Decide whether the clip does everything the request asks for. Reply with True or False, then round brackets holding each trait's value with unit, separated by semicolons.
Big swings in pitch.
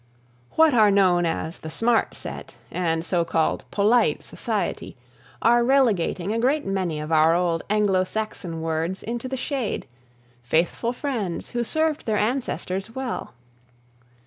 True (6.0 semitones)